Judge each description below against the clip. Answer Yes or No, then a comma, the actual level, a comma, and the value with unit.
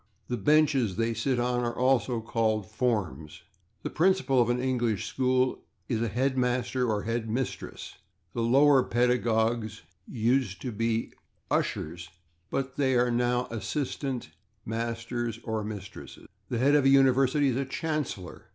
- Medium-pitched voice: No, low, 120 Hz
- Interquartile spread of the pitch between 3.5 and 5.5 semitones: No, average, 2.7 semitones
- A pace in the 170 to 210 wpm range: No, average, 140 wpm